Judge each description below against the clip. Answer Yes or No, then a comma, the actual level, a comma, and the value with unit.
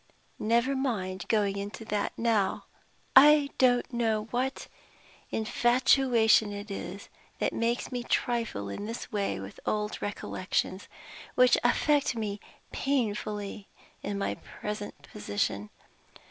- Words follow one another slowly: Yes, slow, 115 wpm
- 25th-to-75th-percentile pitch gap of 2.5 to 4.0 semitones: Yes, average, 3.4 semitones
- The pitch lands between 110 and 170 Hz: No, high, 220 Hz